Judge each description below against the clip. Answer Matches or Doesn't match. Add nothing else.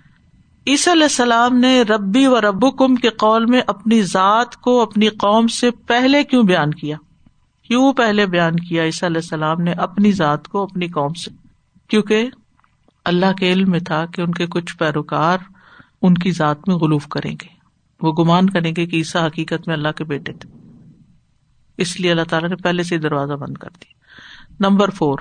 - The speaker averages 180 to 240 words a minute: Matches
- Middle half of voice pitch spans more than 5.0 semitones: Matches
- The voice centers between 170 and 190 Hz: Matches